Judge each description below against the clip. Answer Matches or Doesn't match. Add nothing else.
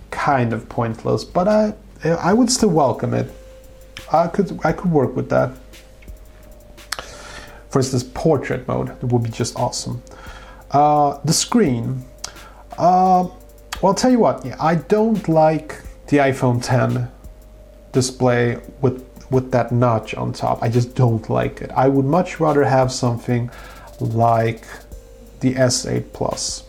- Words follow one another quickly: Doesn't match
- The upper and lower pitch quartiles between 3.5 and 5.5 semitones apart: Matches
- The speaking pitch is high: Doesn't match